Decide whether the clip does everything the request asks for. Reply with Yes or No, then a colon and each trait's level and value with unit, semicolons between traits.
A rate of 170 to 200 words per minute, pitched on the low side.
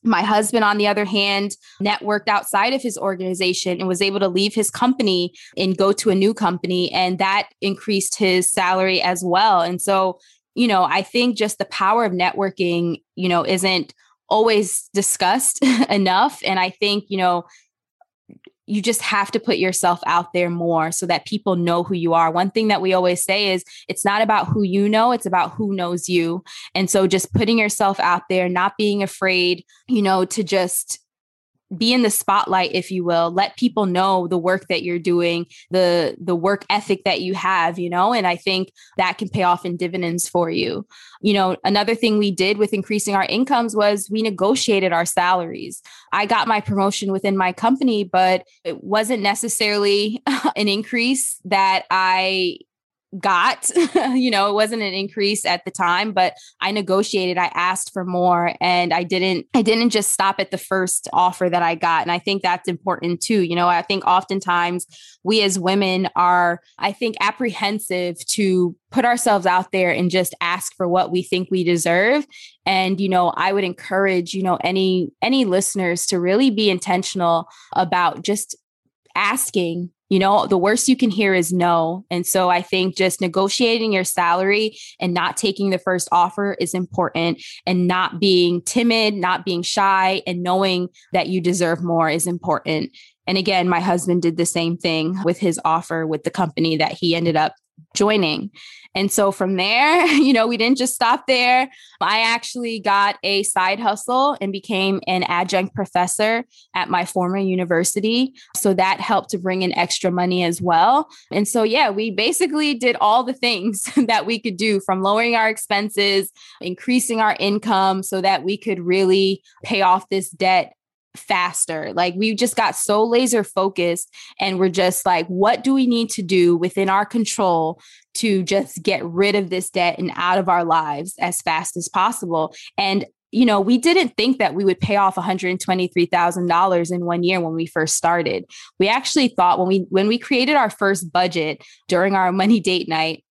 No: average, 185 wpm; high, 190 Hz